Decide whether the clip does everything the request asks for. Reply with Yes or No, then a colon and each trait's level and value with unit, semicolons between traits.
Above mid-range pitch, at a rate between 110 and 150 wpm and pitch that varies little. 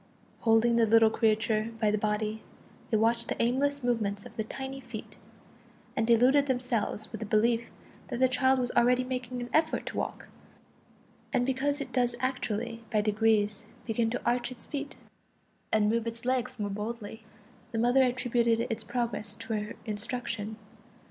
No: high, 235 Hz; average, 165 wpm; narrow, 2.3 semitones